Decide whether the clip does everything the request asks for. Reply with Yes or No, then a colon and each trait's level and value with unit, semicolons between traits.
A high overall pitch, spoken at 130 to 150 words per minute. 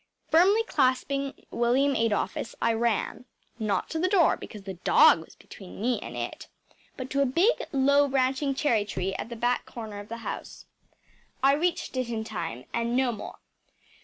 No: high, 245 Hz; average, 175 wpm